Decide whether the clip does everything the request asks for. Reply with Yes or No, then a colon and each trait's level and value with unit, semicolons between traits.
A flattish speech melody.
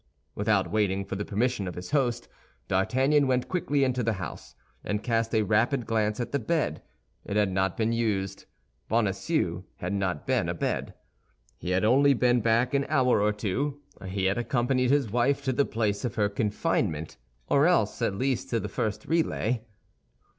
No: average, 4.3 semitones